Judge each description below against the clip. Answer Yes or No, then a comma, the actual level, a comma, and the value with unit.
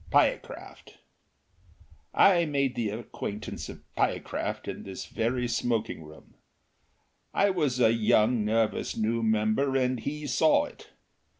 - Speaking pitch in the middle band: No, low, 120 Hz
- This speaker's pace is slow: Yes, slow, 120 wpm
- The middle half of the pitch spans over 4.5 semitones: No, average, 3.9 semitones